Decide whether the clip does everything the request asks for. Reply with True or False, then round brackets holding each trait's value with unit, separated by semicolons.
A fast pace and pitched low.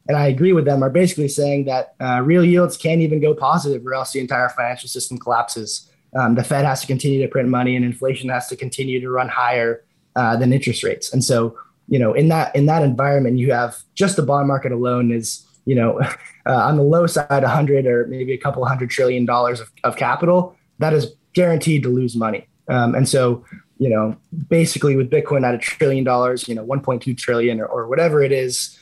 True (225 wpm; 130 Hz)